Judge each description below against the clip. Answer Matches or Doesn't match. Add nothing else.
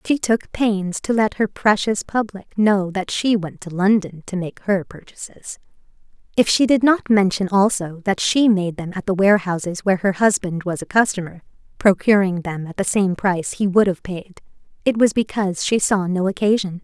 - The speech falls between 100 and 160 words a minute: Doesn't match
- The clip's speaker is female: Matches